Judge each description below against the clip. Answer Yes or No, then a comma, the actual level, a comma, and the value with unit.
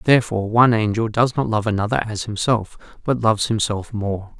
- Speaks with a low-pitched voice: Yes, low, 110 Hz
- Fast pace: No, average, 175 wpm